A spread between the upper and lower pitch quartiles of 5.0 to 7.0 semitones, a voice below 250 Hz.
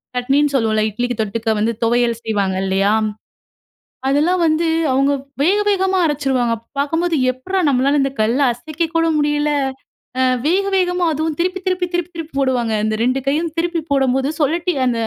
No: wide, 5.4 semitones; very high, 285 Hz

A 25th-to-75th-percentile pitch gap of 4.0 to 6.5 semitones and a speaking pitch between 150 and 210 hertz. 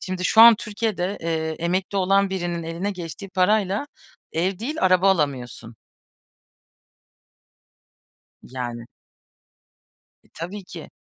No: average, 3.2 semitones; medium, 185 Hz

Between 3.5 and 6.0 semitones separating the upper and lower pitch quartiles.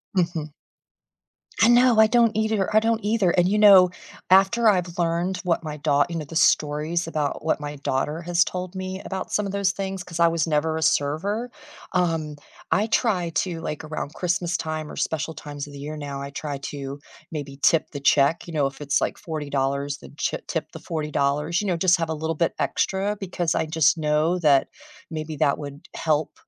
Yes: average, 4.0 semitones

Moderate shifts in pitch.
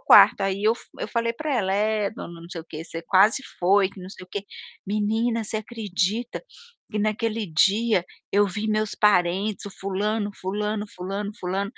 No: narrow, 2.3 semitones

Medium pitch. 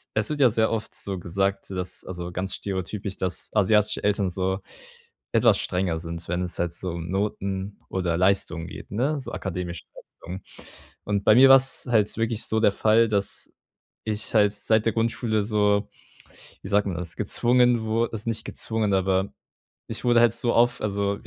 No: low, 100 Hz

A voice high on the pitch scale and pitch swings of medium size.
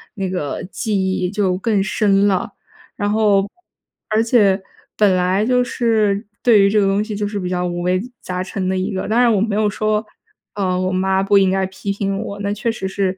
No: high, 200 Hz; narrow, 2.0 semitones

